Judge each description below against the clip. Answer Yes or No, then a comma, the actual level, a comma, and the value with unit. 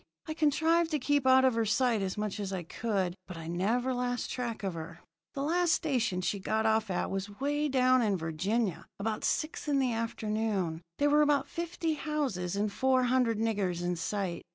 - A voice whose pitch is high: Yes, high, 225 Hz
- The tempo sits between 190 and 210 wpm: Yes, average, 200 wpm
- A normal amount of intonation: No, wide, 6.0 semitones